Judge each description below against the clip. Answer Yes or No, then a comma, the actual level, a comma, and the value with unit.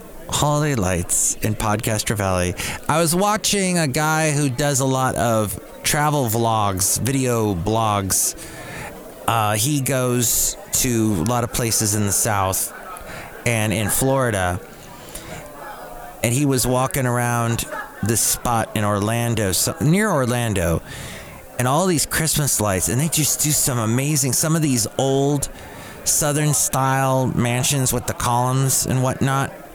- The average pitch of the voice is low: Yes, low, 125 Hz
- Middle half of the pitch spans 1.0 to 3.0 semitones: No, average, 4.3 semitones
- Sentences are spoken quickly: No, slow, 135 wpm